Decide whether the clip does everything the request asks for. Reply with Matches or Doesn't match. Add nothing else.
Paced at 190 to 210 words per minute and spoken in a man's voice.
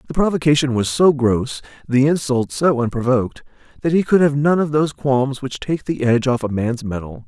Matches